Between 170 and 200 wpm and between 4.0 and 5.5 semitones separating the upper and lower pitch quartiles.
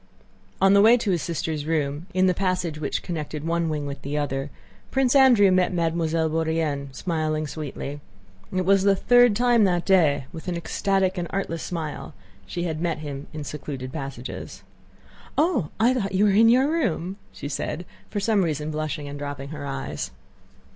Yes: average, 180 wpm; average, 4.6 semitones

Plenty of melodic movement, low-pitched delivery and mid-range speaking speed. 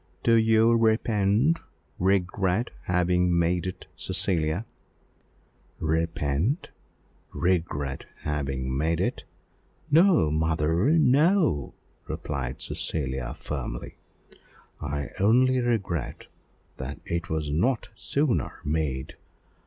No: wide, 7.1 semitones; very low, 85 Hz; slow, 85 wpm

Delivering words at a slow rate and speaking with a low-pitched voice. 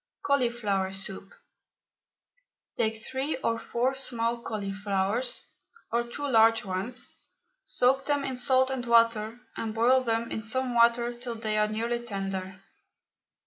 No: slow, 130 wpm; high, 235 Hz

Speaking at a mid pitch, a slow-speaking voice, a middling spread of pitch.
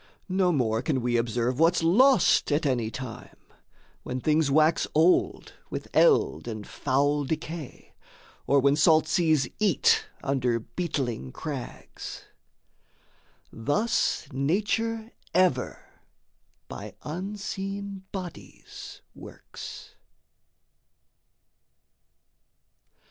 No: medium, 155 Hz; slow, 90 wpm; wide, 6.3 semitones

